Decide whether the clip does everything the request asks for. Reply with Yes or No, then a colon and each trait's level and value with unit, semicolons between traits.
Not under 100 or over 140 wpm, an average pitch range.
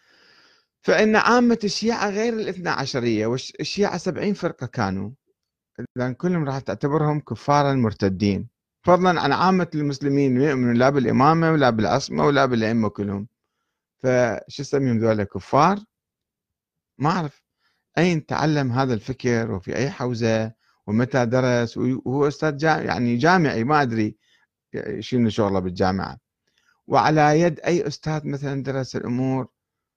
Yes: average, 120 wpm; average, 4.9 semitones